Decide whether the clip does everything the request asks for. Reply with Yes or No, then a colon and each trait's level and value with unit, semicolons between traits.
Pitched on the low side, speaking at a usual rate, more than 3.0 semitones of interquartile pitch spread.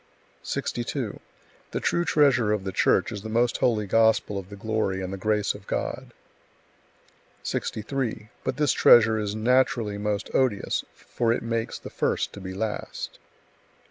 No: low, 110 Hz; average, 155 wpm; average, 2.7 semitones